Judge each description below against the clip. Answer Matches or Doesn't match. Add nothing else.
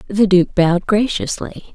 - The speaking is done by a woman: Matches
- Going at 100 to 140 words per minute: Matches